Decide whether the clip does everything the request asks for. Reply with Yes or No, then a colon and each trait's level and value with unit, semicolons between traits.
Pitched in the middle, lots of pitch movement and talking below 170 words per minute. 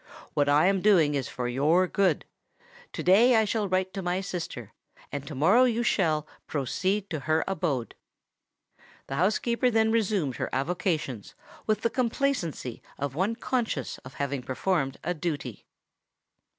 Yes: medium, 175 Hz; wide, 6.6 semitones; average, 150 wpm